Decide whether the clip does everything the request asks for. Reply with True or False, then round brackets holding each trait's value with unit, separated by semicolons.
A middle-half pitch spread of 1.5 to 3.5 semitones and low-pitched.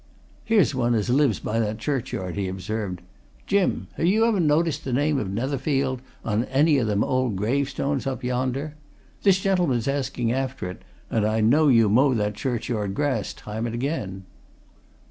False (4.7 semitones; 130 Hz)